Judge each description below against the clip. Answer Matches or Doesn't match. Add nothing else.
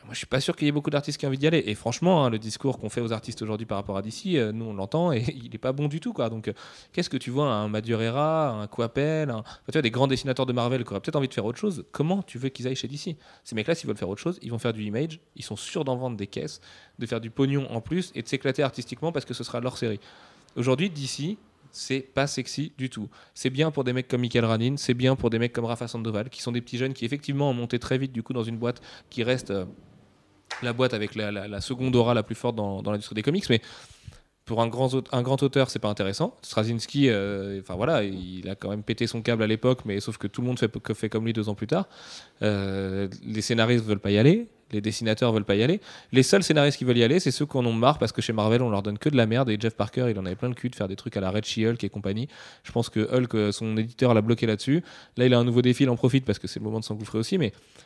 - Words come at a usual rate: Doesn't match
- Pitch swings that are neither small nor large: Matches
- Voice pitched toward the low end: Matches